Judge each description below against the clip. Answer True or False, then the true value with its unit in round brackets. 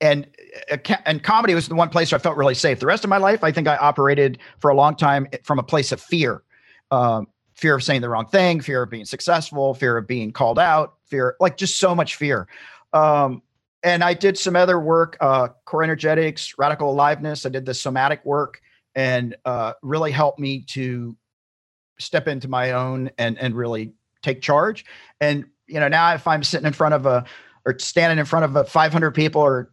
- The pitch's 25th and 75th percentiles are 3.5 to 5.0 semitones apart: True (4.1 semitones)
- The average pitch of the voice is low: False (145 Hz)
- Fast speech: True (210 wpm)